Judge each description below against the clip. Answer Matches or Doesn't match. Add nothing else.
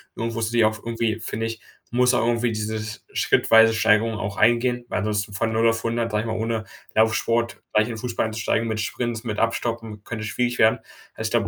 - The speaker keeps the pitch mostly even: Matches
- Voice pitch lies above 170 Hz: Doesn't match